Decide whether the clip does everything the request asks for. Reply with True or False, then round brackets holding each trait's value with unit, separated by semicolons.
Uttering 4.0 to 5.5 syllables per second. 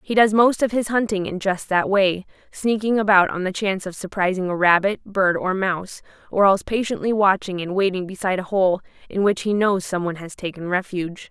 False (5.7 syllables/s)